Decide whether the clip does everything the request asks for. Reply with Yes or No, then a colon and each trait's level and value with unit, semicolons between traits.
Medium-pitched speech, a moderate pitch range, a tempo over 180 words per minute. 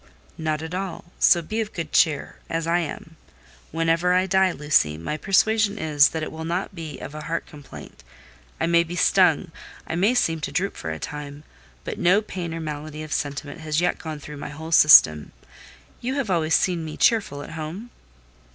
Yes: medium, 165 Hz; average, 3.0 semitones; average, 190 wpm